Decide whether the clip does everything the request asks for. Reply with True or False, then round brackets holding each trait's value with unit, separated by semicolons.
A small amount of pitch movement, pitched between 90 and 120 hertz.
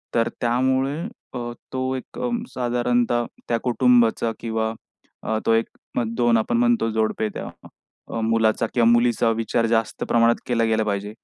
True (1.3 semitones; 115 Hz)